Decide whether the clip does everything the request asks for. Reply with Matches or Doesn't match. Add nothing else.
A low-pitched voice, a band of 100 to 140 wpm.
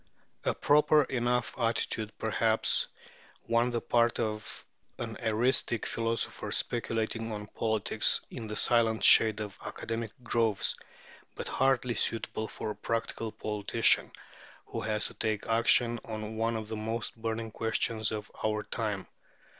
Matches